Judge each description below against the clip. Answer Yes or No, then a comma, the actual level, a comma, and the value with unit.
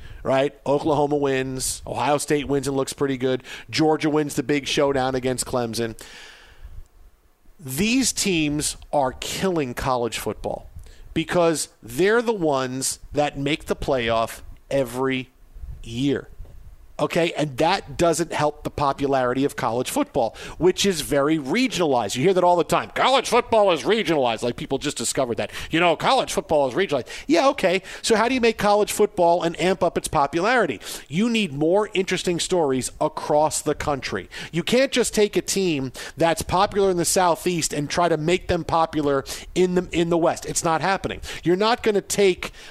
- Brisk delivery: No, average, 170 wpm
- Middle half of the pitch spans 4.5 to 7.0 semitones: Yes, average, 5.3 semitones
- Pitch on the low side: No, medium, 155 Hz